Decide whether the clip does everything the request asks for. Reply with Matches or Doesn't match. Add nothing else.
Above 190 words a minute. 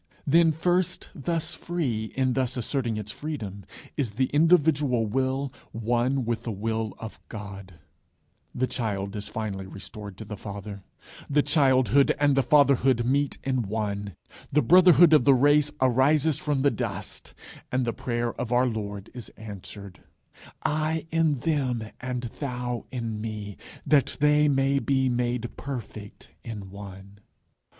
Doesn't match